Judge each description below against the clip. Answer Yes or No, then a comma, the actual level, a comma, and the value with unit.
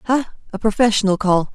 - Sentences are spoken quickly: No, average, 155 wpm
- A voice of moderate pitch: No, high, 210 Hz